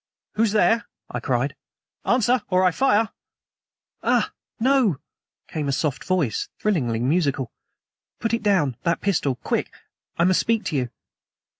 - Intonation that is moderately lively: No, wide, 7.7 semitones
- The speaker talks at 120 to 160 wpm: Yes, average, 140 wpm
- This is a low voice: No, medium, 185 Hz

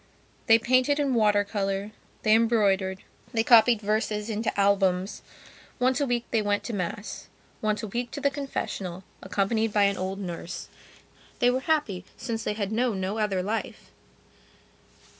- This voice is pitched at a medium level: No, high, 215 Hz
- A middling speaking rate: Yes, average, 160 wpm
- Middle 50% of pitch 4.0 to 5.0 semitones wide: No, average, 3.2 semitones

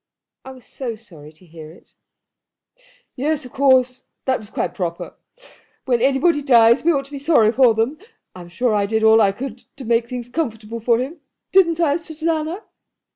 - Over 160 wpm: Yes, average, 180 wpm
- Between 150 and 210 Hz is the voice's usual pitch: No, very high, 250 Hz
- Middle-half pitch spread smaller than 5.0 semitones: Yes, average, 4.5 semitones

